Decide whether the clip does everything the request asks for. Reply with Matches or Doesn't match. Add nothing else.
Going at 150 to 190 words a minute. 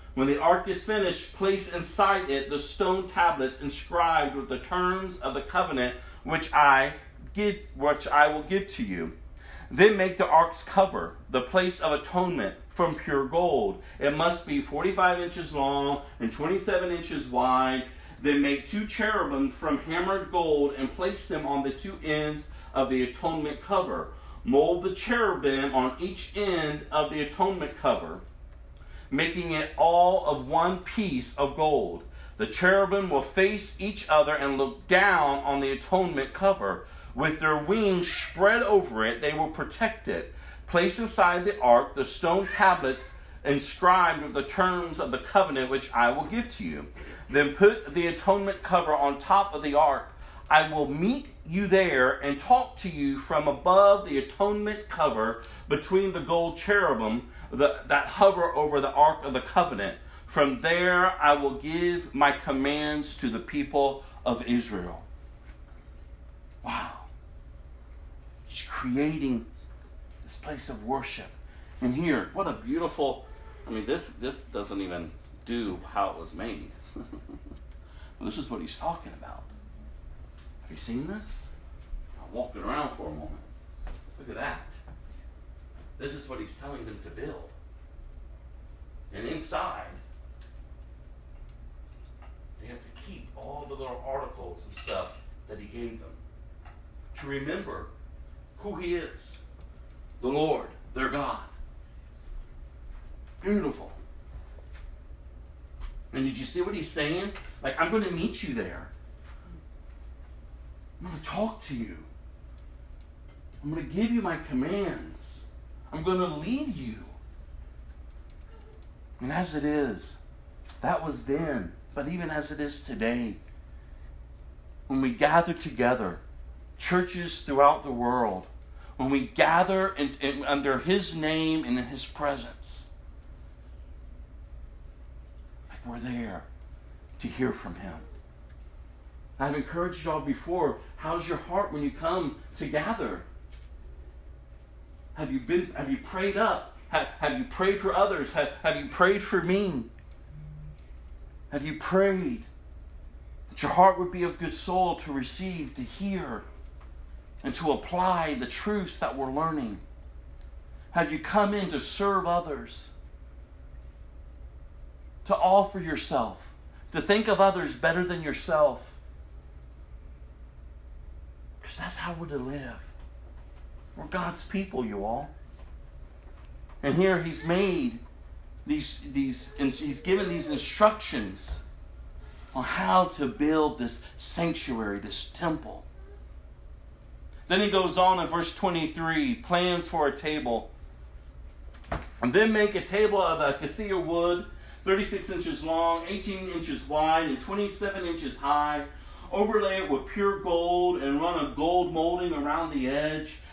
Doesn't match